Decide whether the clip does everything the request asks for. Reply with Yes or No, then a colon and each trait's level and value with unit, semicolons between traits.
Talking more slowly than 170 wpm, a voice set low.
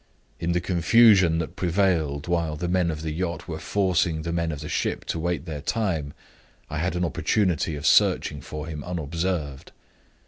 No: average, 180 wpm; very low, 85 Hz